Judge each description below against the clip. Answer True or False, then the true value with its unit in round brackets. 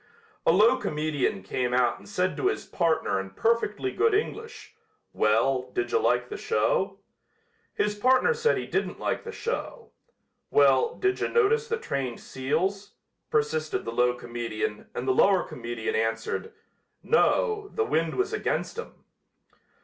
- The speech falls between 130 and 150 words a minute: True (145 wpm)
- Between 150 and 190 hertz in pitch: True (185 Hz)